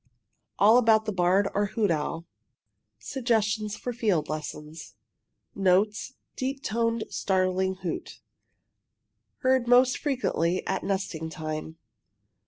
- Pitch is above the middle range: Yes, high, 200 Hz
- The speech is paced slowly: Yes, slow, 105 wpm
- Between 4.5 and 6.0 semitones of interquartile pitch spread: Yes, average, 4.9 semitones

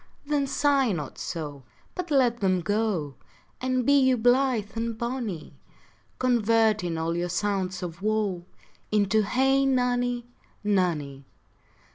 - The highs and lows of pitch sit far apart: Yes, wide, 5.7 semitones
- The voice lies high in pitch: Yes, high, 220 Hz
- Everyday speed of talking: No, slow, 120 wpm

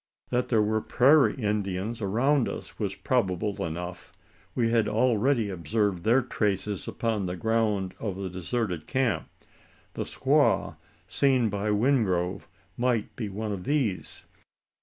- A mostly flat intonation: No, average, 3.8 semitones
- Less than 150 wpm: Yes, slow, 135 wpm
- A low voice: Yes, low, 105 Hz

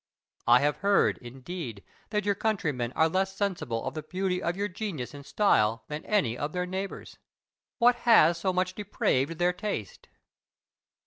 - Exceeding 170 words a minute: No, average, 165 wpm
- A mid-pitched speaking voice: Yes, medium, 180 Hz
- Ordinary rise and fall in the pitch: No, wide, 6.1 semitones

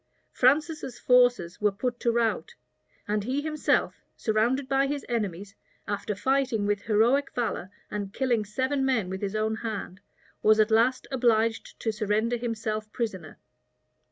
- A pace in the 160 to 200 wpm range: No, average, 145 wpm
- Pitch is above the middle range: Yes, high, 225 Hz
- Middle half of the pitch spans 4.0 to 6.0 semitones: No, average, 3.6 semitones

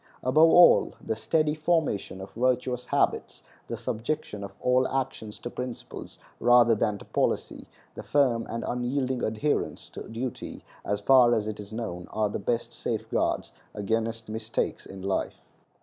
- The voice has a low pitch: Yes, low, 115 Hz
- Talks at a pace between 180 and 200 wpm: No, average, 150 wpm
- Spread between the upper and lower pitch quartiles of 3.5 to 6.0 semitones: No, average, 3.1 semitones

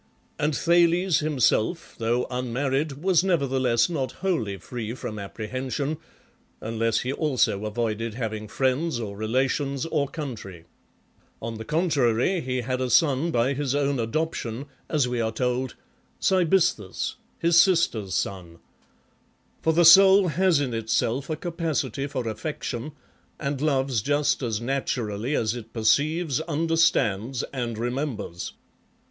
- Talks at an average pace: No, slow, 130 wpm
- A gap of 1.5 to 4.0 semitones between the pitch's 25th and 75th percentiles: No, average, 5.2 semitones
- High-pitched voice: No, low, 130 Hz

